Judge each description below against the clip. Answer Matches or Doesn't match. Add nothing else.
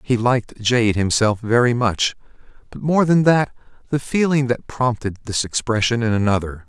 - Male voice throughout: Matches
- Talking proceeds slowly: Doesn't match